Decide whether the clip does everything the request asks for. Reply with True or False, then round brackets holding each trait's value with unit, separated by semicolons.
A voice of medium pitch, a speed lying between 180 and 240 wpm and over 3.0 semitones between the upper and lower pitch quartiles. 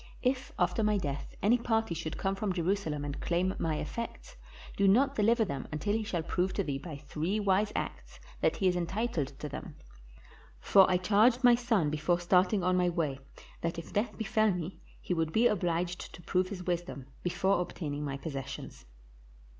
True (180 Hz; 185 wpm; 4.5 semitones)